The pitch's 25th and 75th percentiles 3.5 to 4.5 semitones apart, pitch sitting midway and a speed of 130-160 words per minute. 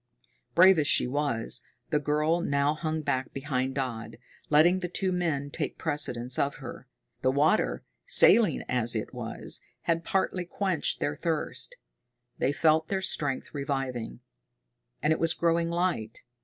Yes: average, 4.2 semitones; medium, 150 Hz; average, 145 wpm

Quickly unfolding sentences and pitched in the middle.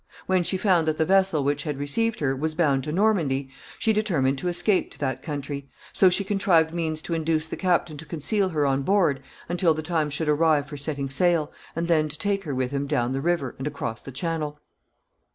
Yes: fast, 220 wpm; medium, 155 Hz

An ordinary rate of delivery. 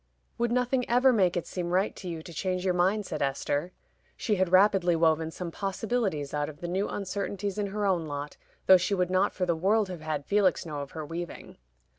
No: fast, 220 wpm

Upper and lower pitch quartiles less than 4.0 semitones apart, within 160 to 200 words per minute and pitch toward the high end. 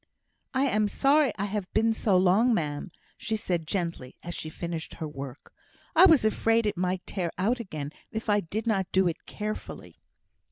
No: average, 4.5 semitones; average, 185 wpm; high, 195 Hz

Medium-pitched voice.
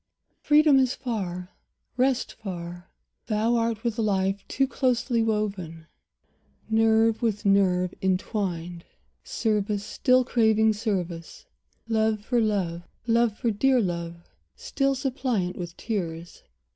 No: high, 215 Hz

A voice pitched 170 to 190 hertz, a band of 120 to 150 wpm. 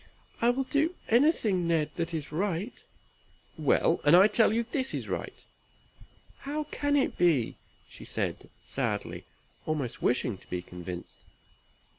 Yes: medium, 185 Hz; average, 140 wpm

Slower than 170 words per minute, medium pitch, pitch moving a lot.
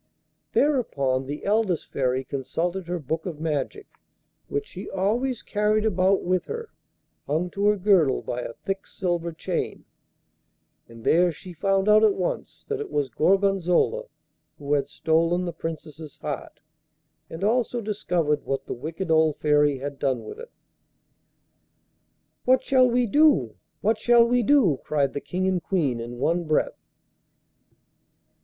Yes: average, 150 wpm; medium, 175 Hz; wide, 6.2 semitones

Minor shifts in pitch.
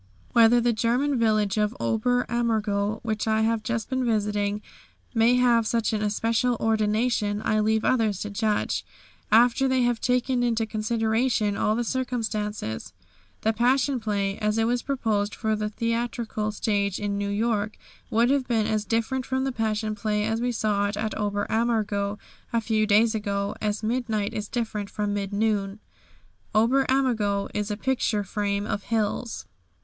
Yes: narrow, 2.1 semitones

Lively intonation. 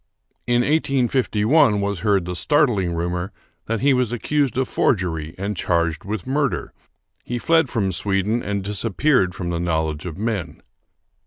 Yes: wide, 5.7 semitones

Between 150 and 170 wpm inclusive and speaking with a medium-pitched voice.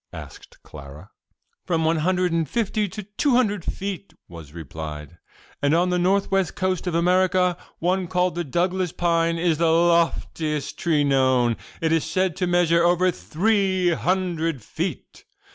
Yes: average, 155 wpm; medium, 175 Hz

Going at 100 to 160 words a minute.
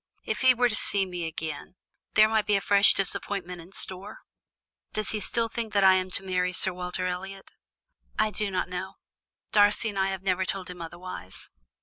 No: average, 195 wpm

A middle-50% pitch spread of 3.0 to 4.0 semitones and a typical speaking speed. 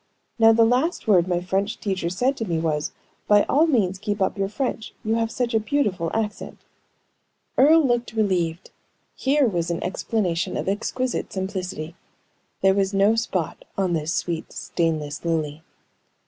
No: average, 4.7 semitones; average, 160 wpm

